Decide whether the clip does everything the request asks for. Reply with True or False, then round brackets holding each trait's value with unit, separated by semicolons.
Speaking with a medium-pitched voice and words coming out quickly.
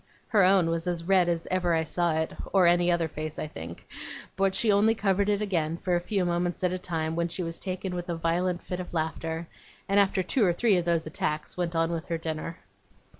True (175 Hz; 235 wpm)